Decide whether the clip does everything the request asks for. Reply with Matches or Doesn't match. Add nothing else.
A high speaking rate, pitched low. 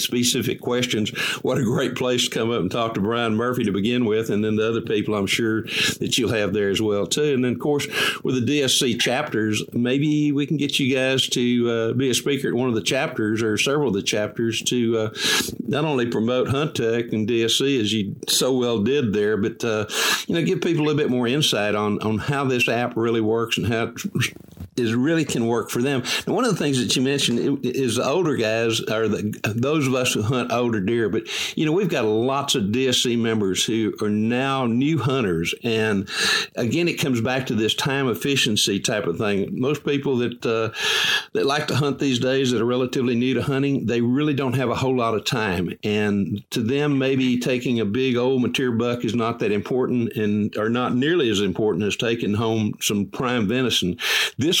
Matches